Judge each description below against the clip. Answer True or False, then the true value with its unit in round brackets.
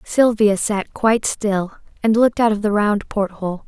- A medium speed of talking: True (195 wpm)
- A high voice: True (210 Hz)